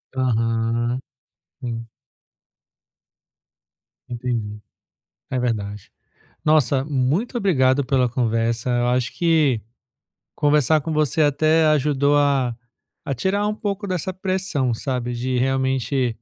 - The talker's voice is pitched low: Yes, low, 130 Hz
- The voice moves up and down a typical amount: Yes, average, 4.1 semitones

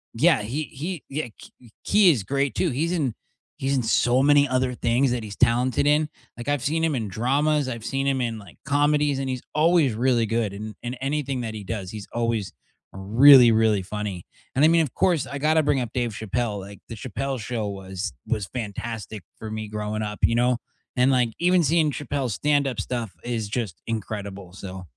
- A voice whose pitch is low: Yes, low, 120 Hz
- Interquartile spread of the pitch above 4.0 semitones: Yes, average, 4.7 semitones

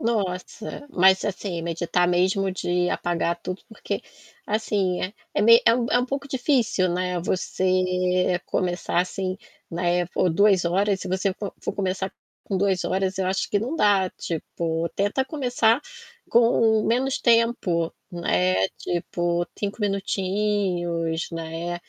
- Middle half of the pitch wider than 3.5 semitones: No, average, 3.2 semitones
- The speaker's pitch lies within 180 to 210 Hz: Yes, medium, 185 Hz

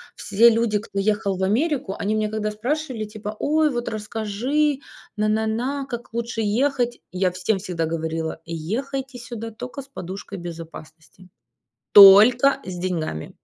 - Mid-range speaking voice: No, high, 215 Hz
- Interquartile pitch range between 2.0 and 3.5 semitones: No, average, 4.4 semitones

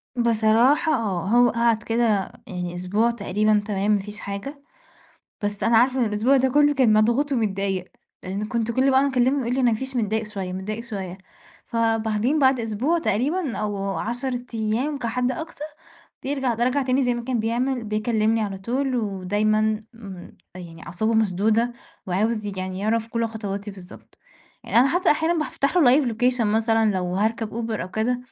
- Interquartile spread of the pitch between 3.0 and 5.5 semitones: Yes, average, 3.4 semitones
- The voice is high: Yes, high, 225 Hz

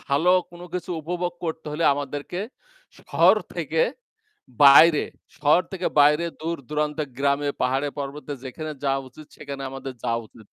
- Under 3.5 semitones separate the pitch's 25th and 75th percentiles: Yes, average, 2.7 semitones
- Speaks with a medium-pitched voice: Yes, medium, 145 Hz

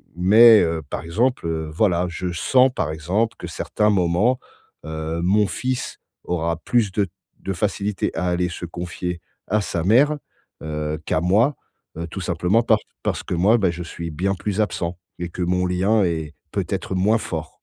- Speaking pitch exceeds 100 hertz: No, very low, 90 Hz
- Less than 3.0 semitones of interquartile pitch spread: No, average, 4.0 semitones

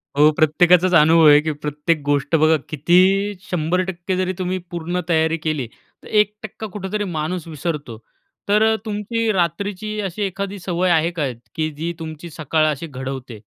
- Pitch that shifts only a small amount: No, average, 3.4 semitones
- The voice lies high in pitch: No, medium, 170 Hz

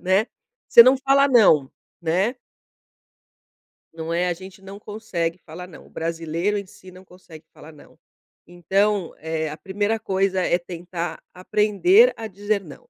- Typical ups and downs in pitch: Yes, average, 3.7 semitones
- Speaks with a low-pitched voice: No, medium, 185 Hz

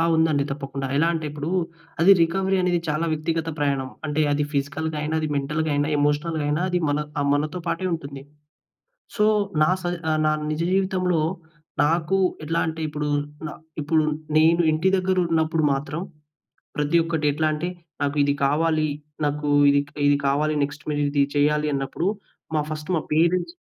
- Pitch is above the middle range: No, medium, 155 Hz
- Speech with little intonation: Yes, narrow, 2.1 semitones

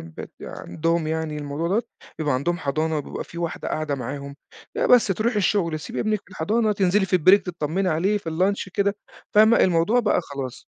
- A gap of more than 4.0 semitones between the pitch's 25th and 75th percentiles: Yes, average, 4.6 semitones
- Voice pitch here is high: No, medium, 170 Hz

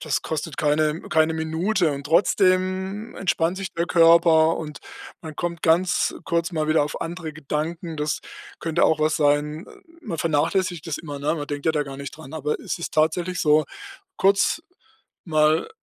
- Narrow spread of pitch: Yes, narrow, 2.3 semitones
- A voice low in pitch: No, medium, 160 Hz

